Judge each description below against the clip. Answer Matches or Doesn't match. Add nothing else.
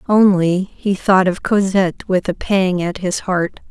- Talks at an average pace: Matches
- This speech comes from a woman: Matches